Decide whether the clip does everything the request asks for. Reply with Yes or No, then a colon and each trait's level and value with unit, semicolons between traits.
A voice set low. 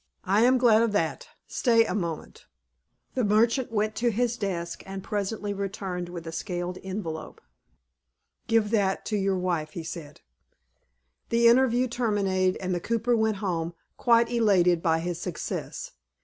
No: high, 200 Hz